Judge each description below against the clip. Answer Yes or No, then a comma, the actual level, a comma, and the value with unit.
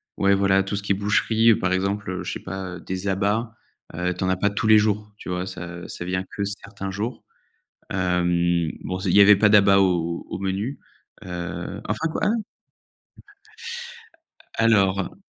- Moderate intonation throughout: No, narrow, 1.9 semitones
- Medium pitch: No, very low, 95 Hz